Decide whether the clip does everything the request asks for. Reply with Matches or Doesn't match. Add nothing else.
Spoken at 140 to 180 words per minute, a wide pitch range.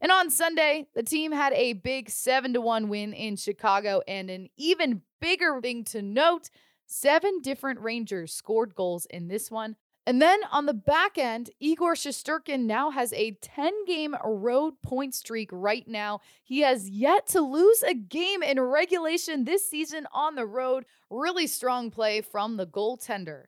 Matches